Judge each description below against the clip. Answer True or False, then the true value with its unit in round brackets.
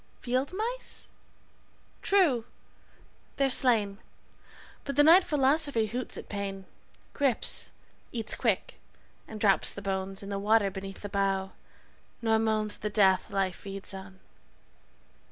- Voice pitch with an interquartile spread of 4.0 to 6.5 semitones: True (5.0 semitones)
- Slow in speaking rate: True (130 wpm)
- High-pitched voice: True (215 Hz)